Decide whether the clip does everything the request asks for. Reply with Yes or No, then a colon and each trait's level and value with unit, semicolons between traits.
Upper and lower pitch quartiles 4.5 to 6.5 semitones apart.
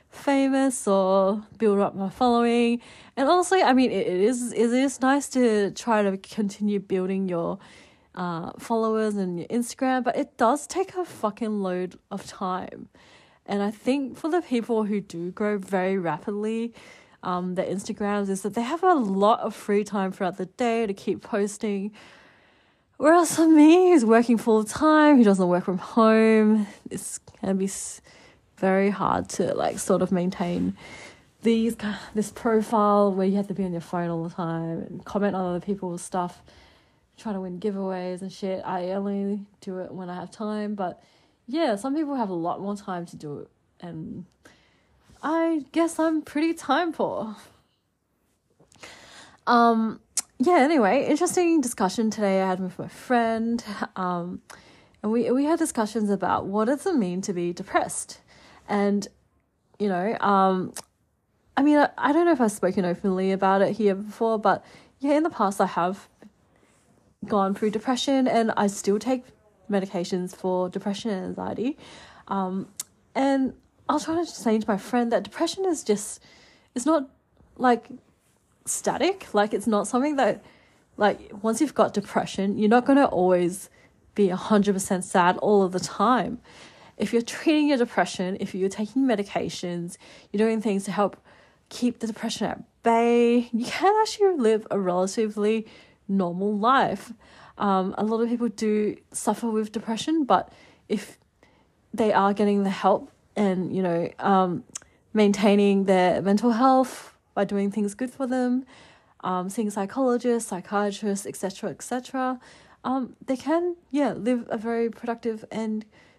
No: average, 4.0 semitones